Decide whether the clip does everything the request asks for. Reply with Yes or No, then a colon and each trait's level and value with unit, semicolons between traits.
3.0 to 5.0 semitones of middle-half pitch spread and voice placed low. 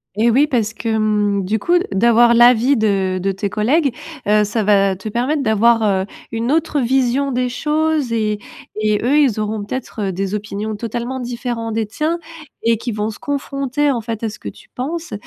No: average, 3.7 semitones; high, 230 Hz